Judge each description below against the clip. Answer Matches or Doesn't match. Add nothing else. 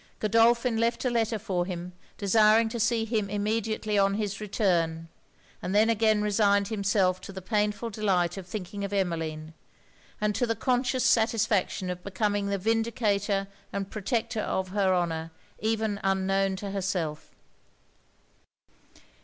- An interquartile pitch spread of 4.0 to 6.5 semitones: Doesn't match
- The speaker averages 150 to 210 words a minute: Doesn't match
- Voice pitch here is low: Doesn't match